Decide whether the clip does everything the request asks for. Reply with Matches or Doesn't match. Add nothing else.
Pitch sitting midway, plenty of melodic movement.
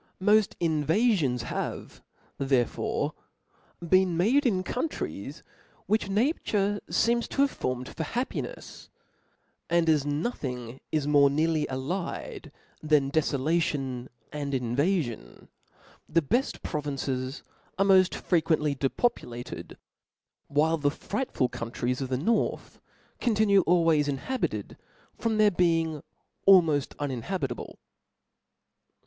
Matches